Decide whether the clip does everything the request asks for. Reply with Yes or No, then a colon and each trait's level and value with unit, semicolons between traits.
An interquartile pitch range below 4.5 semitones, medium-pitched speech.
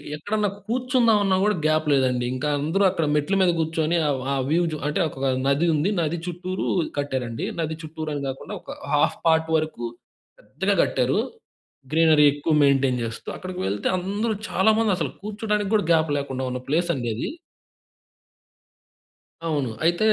No: average, 5.1 semitones; medium, 160 Hz